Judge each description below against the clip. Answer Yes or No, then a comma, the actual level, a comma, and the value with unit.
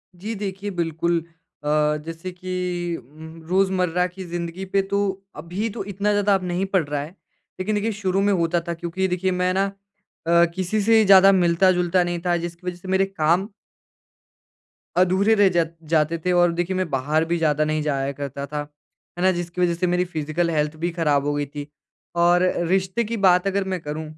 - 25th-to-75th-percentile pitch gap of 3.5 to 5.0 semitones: No, average, 2.7 semitones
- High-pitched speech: No, medium, 175 Hz